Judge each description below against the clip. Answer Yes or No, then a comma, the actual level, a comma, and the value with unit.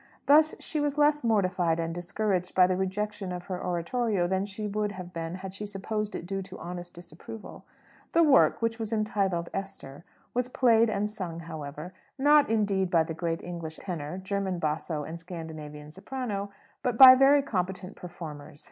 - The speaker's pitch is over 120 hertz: Yes, high, 190 Hz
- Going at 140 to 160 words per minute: No, average, 175 wpm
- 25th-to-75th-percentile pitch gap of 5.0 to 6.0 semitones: No, average, 4.1 semitones